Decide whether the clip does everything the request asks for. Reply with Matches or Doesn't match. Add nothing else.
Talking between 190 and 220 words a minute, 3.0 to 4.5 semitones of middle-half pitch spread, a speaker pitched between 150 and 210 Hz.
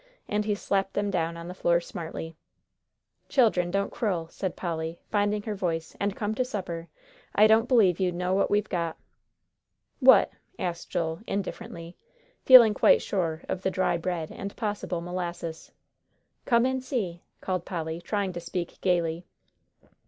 Doesn't match